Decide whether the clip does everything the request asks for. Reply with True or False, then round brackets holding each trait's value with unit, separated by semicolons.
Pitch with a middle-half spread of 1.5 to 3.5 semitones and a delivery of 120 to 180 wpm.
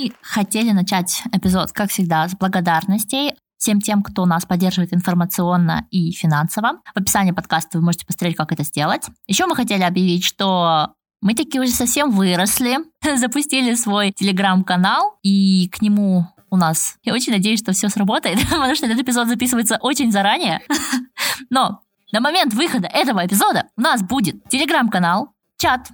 False (5.2 semitones; 155 wpm)